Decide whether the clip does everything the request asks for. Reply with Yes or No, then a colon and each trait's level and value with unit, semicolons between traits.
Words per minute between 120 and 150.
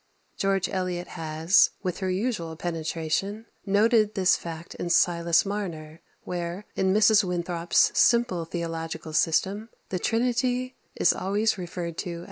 Yes: slow, 135 wpm